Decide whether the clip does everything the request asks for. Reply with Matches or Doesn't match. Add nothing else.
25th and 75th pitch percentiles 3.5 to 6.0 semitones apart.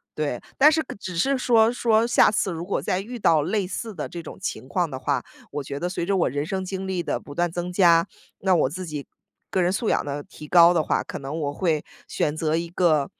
Matches